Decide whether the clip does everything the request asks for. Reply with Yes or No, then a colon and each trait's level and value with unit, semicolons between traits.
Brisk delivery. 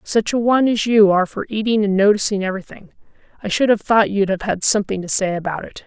Yes: fast, 235 wpm